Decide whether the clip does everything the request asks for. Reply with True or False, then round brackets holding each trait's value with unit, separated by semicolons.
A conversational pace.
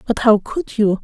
False (230 wpm)